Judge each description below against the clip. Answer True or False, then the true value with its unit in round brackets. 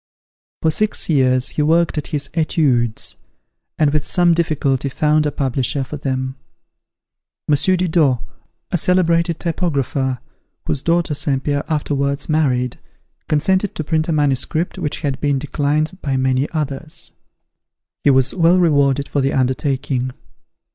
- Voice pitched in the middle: True (145 Hz)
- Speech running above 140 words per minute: False (135 wpm)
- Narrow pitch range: False (3.1 semitones)